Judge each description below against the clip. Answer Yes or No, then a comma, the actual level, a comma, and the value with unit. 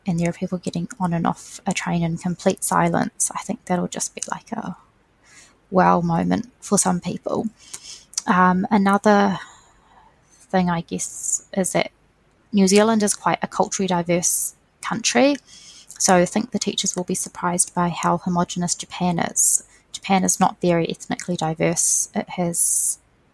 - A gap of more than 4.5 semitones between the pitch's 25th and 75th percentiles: No, narrow, 2.5 semitones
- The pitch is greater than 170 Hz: Yes, medium, 185 Hz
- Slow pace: No, average, 155 wpm